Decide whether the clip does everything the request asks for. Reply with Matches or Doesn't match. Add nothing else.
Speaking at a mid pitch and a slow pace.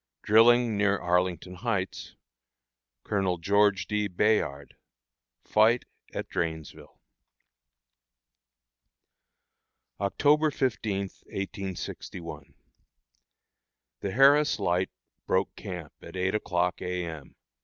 Doesn't match